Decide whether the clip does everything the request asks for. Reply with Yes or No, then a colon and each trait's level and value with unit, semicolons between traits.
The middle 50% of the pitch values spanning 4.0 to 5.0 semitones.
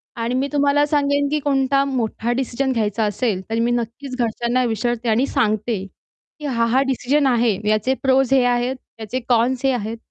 No: average, 2.7 semitones